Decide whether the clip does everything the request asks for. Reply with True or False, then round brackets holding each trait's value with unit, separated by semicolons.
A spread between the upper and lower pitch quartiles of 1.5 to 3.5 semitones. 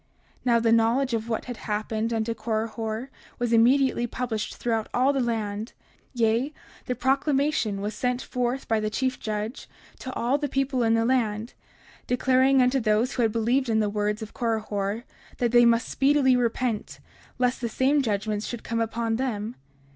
True (2.7 semitones)